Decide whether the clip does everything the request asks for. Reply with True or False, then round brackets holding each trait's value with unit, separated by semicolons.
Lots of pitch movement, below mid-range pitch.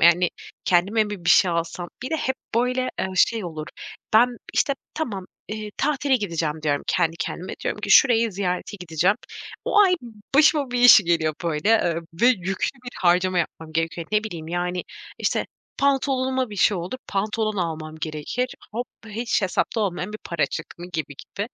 False (5.9 semitones; 195 Hz)